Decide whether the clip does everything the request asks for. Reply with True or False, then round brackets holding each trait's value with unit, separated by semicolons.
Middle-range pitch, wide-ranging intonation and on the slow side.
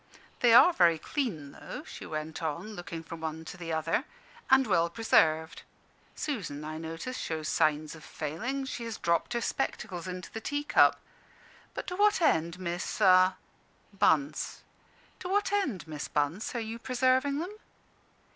False (175 Hz; 8.1 semitones; 155 wpm)